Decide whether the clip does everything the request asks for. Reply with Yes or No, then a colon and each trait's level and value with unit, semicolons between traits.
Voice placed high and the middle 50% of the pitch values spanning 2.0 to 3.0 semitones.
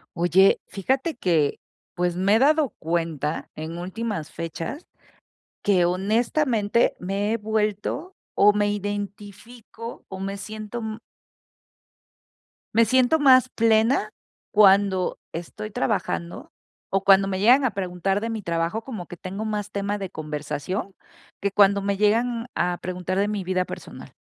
No: high, 200 Hz; average, 3.4 semitones